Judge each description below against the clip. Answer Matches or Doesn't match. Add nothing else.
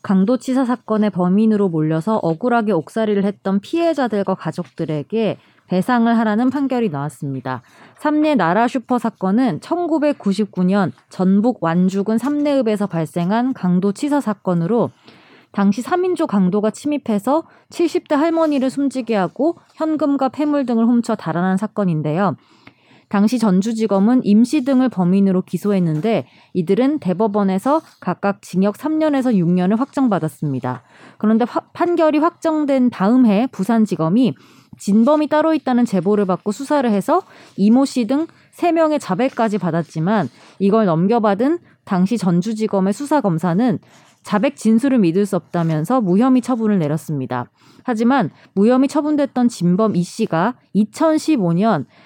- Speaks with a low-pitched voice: Doesn't match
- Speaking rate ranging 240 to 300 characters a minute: Doesn't match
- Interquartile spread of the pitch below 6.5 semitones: Matches